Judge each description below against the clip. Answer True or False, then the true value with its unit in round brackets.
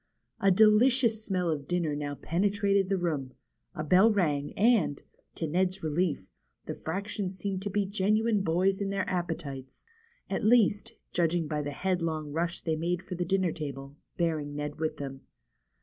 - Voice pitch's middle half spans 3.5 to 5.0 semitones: True (4.4 semitones)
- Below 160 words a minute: False (165 wpm)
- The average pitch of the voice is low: False (175 Hz)